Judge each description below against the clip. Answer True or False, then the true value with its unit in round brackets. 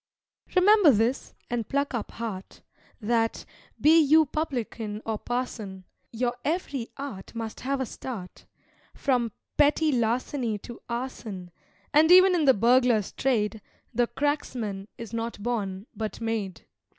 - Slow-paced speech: True (130 wpm)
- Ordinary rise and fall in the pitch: True (4.1 semitones)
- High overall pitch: True (240 Hz)